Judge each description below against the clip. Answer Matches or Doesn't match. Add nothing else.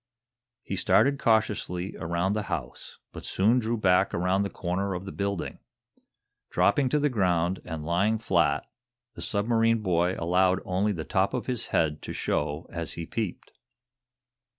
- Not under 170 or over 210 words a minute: Doesn't match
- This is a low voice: Matches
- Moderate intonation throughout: Matches